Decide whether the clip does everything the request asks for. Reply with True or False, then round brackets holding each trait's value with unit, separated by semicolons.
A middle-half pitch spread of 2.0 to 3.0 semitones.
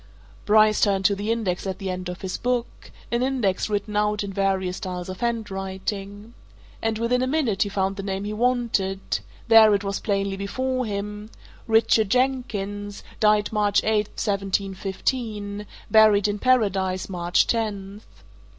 True (2.4 semitones)